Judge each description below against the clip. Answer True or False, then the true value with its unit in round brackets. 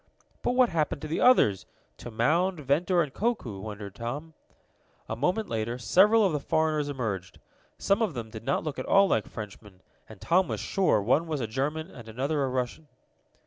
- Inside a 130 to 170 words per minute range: False (190 wpm)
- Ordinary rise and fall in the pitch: False (7.3 semitones)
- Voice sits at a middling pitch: True (145 Hz)